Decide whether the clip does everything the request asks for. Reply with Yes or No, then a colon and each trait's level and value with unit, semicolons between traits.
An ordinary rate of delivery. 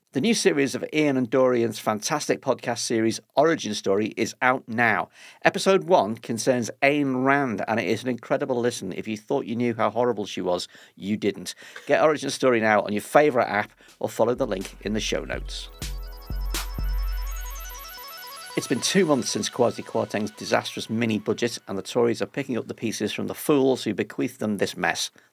Yes: average, 185 wpm